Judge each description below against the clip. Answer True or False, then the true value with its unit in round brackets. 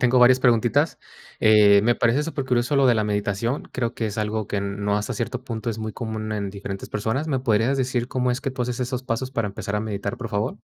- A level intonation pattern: False (3.3 semitones)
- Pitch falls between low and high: False (115 Hz)